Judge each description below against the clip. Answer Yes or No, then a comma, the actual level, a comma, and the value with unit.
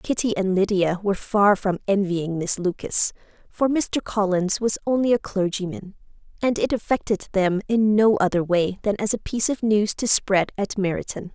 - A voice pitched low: No, high, 200 Hz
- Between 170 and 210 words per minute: Yes, average, 180 wpm